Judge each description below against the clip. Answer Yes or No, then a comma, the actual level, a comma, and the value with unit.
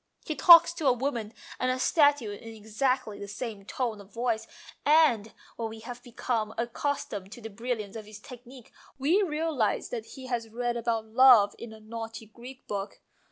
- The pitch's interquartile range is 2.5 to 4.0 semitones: Yes, average, 3.0 semitones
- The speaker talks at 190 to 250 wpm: Yes, average, 195 wpm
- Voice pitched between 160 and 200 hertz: No, high, 235 Hz